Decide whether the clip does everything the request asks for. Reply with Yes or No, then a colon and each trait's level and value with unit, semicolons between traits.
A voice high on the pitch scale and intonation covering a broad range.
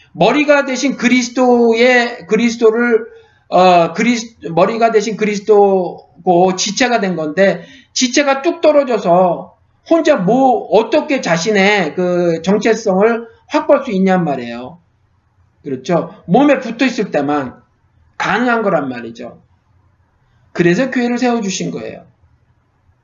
Yes: high, 205 Hz; wide, 6.9 semitones